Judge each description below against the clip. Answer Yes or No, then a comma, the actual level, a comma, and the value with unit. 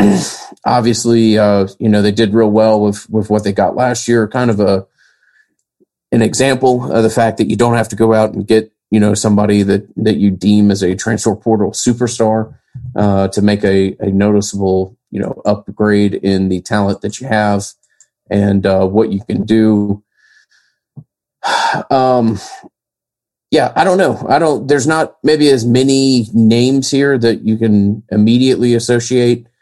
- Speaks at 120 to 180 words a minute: Yes, average, 170 wpm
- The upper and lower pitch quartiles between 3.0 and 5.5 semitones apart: No, narrow, 2.6 semitones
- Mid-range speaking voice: No, low, 110 Hz